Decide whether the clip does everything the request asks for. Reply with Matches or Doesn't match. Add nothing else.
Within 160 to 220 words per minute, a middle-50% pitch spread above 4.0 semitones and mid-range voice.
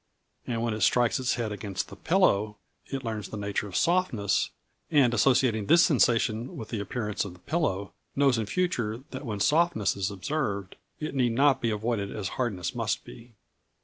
Doesn't match